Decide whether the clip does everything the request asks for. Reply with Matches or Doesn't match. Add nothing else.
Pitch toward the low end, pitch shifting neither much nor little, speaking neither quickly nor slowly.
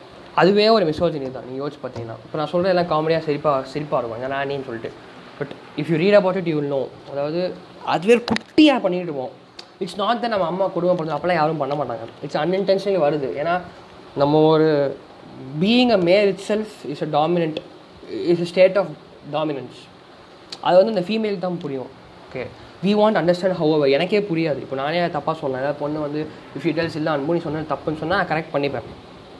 Doesn't match